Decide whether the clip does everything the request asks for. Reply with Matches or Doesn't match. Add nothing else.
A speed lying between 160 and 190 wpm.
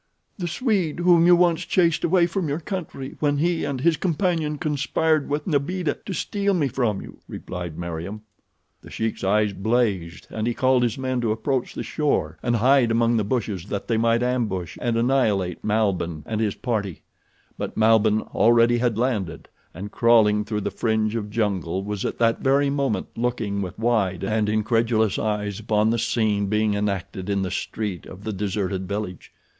Matches